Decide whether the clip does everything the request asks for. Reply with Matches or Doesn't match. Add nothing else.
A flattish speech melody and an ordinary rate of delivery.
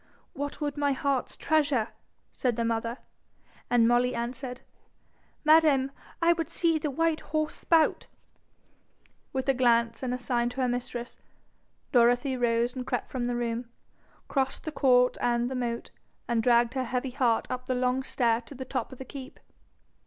Matches